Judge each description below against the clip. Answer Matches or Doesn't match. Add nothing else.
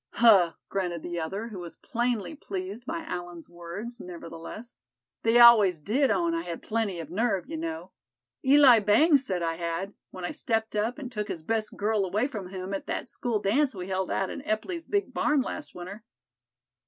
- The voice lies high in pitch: Matches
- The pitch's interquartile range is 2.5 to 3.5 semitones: Doesn't match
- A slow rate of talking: Doesn't match